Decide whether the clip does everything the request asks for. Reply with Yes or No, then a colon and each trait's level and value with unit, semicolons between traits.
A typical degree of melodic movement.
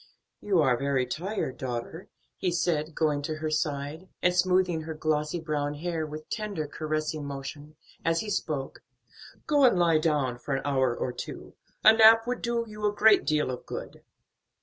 Yes: average, 4.0 semitones